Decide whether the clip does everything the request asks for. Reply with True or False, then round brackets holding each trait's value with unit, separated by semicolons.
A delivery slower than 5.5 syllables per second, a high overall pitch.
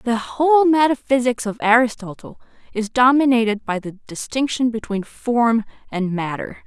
True (4.7 syllables/s; 235 Hz)